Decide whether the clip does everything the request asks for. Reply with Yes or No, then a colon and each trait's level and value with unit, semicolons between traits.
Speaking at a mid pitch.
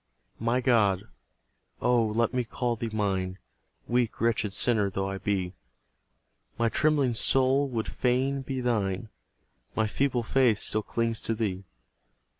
No: low, 115 Hz